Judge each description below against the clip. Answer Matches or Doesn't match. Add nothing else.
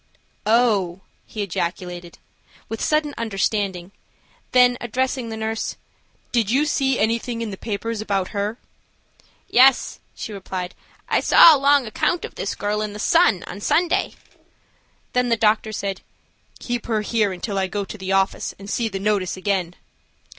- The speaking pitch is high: Matches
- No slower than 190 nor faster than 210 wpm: Doesn't match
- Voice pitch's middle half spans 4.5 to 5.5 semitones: Doesn't match